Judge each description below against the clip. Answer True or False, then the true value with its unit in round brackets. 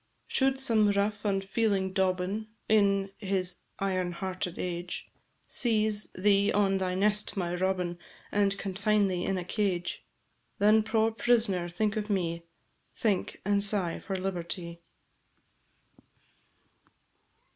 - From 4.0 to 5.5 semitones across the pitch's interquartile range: False (2.4 semitones)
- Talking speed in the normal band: False (115 wpm)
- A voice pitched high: True (195 Hz)